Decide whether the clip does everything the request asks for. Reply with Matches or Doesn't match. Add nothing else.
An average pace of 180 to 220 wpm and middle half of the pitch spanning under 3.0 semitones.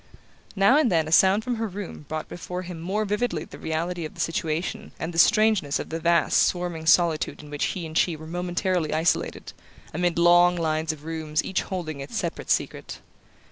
Matches